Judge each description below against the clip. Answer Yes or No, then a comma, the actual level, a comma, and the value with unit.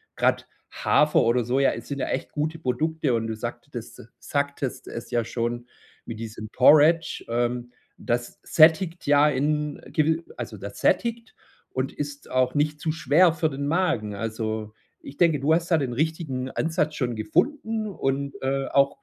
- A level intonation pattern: No, average, 4.6 semitones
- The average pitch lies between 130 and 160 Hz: Yes, medium, 140 Hz